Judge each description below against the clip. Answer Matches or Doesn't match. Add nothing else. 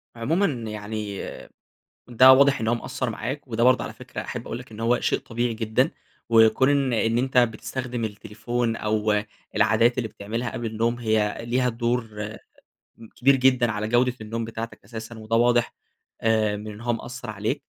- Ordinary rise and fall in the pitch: Doesn't match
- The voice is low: Matches